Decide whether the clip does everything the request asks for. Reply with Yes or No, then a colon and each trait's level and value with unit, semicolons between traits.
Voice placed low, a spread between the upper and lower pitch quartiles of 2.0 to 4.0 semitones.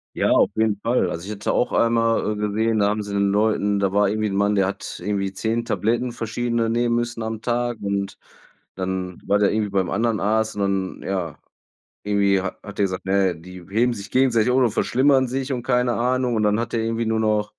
Yes: low, 105 Hz; average, 2.8 semitones